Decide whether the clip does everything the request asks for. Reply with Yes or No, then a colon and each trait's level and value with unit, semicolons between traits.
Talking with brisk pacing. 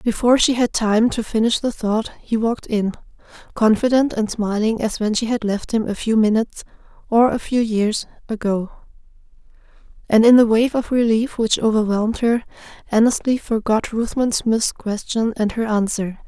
No: average, 160 wpm